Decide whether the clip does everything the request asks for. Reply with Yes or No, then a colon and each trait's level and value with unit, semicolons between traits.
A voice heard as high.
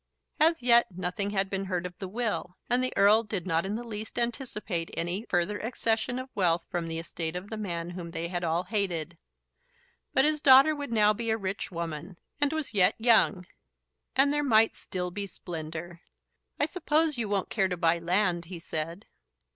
Yes: high, 195 Hz